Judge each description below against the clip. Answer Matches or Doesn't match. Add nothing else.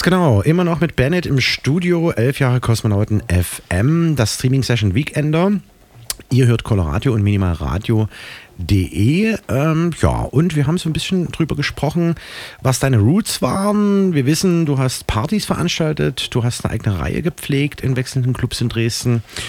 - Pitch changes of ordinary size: Doesn't match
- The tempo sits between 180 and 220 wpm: Doesn't match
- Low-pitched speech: Matches